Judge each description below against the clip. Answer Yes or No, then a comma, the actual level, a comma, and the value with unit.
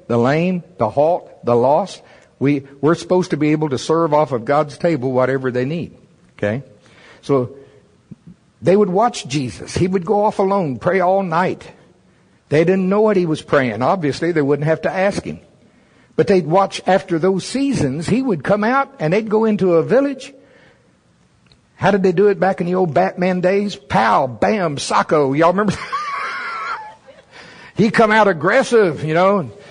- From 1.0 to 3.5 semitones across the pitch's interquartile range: No, average, 5.2 semitones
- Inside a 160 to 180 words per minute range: Yes, average, 175 wpm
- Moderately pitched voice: Yes, medium, 180 Hz